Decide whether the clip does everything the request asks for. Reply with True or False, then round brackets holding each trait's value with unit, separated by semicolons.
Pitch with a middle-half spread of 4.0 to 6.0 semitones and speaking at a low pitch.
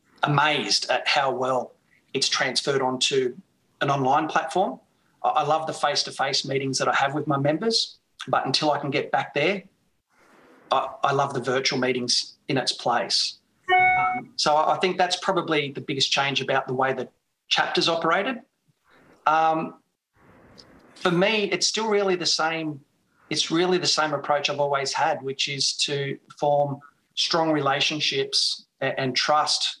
False (4.7 semitones; 150 Hz)